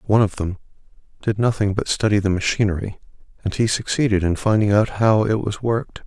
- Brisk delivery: No, average, 190 wpm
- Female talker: No, male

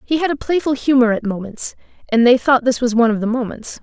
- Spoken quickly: Yes, fast, 250 wpm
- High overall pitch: Yes, high, 245 Hz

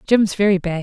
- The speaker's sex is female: Yes, female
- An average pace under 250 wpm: Yes, fast, 220 wpm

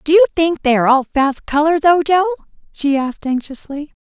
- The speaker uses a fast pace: No, average, 180 wpm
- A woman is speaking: Yes, female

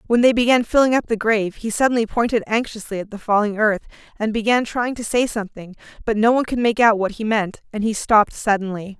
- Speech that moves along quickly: Yes, fast, 225 wpm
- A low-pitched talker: No, high, 220 Hz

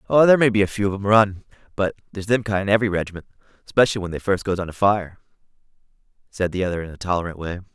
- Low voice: Yes, low, 100 Hz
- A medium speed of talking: No, fast, 230 wpm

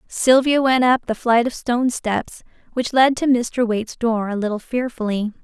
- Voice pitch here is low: No, high, 240 Hz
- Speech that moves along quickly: No, average, 190 wpm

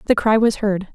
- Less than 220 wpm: No, fast, 255 wpm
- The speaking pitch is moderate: No, high, 210 Hz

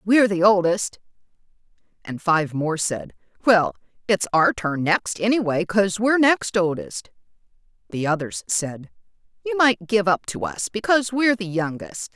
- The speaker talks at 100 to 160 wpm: Yes, average, 150 wpm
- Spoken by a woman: Yes, female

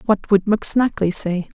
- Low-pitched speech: No, high, 200 Hz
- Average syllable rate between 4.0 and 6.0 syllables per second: Yes, 5.2 syllables/s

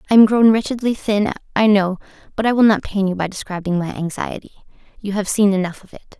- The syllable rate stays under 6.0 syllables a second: No, 6.1 syllables/s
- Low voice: No, high, 200 Hz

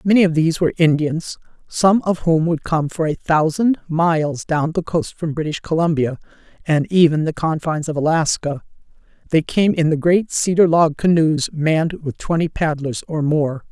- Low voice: No, medium, 160 Hz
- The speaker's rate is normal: Yes, average, 175 wpm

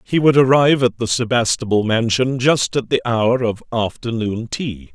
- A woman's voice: No, male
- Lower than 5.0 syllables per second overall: Yes, 4.7 syllables/s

